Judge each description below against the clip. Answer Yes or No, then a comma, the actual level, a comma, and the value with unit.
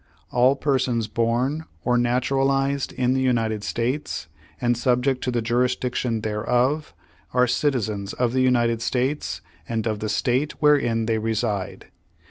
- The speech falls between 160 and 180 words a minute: No, slow, 135 wpm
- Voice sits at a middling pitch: No, low, 125 Hz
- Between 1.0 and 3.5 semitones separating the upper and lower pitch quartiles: Yes, narrow, 2.4 semitones